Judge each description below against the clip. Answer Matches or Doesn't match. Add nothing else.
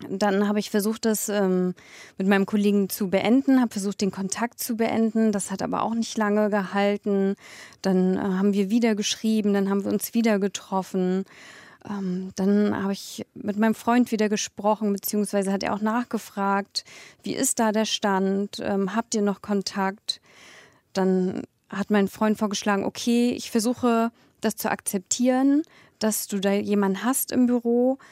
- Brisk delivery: Doesn't match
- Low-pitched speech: Doesn't match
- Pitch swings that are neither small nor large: Doesn't match